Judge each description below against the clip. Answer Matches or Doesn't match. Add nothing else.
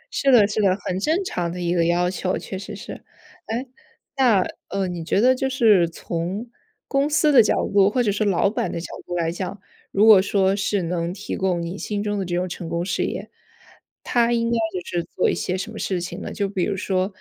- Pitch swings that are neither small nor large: Matches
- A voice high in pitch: Matches